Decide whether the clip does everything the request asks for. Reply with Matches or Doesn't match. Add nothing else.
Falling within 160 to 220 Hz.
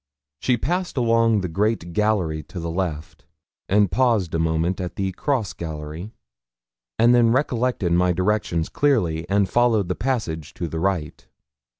Doesn't match